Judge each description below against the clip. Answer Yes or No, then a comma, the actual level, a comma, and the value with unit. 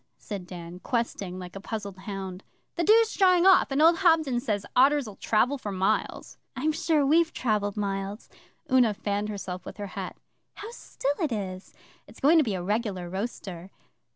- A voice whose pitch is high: Yes, high, 215 Hz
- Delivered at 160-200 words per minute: Yes, average, 175 wpm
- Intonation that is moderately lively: No, wide, 6.9 semitones